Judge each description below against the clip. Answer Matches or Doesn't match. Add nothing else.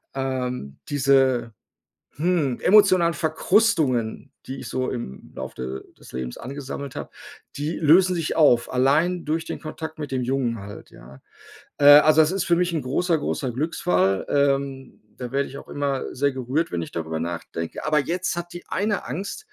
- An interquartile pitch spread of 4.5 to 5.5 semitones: Matches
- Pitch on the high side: Doesn't match